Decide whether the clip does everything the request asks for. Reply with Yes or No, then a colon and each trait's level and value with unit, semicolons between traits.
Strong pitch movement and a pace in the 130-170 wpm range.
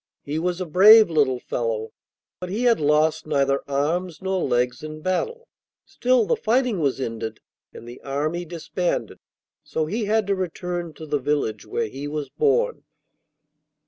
Yes: wide, 5.9 semitones; average, 160 wpm